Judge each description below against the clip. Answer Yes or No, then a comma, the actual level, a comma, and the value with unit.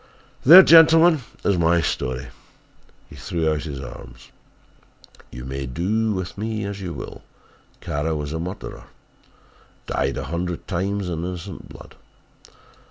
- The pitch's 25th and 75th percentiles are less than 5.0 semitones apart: No, wide, 5.4 semitones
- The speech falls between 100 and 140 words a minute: Yes, slow, 135 wpm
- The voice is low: Yes, very low, 85 Hz